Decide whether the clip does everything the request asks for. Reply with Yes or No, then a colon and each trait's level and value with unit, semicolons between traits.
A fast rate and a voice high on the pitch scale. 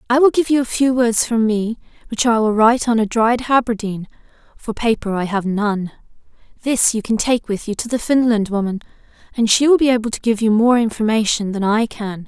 Yes: fast, 220 wpm; high, 225 Hz